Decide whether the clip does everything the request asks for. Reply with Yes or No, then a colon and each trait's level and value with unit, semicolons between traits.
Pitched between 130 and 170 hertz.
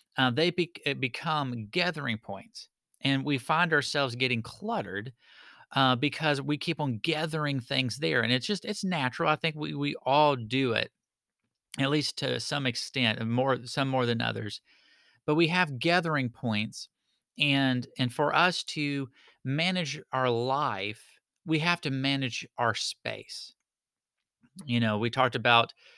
Yes: low, 135 Hz